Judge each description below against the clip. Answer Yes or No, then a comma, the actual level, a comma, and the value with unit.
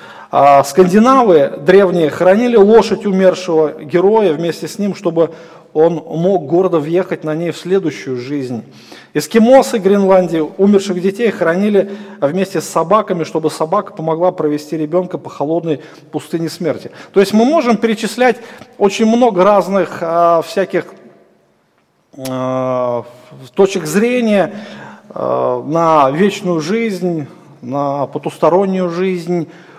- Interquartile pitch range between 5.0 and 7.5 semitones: No, average, 4.1 semitones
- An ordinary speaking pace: No, slow, 105 wpm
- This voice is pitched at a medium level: Yes, medium, 175 Hz